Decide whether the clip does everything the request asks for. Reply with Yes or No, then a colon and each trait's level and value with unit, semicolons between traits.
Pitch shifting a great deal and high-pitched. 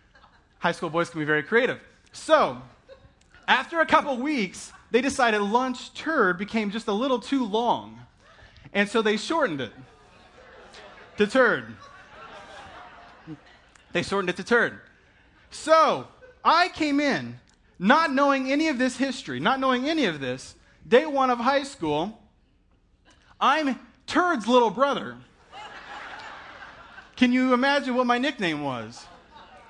Yes: wide, 5.9 semitones; very high, 250 Hz